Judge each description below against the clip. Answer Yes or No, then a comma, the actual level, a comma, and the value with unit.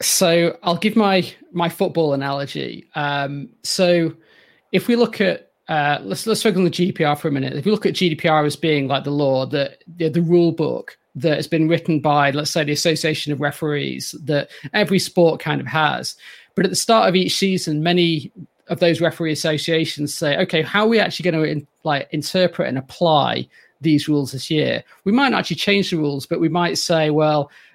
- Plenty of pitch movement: No, average, 3.2 semitones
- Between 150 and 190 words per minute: No, fast, 205 wpm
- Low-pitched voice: No, medium, 165 Hz